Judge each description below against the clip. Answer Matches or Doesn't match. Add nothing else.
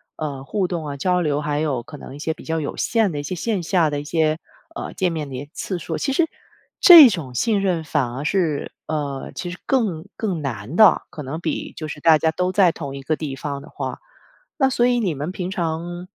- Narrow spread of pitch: Doesn't match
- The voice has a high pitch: Doesn't match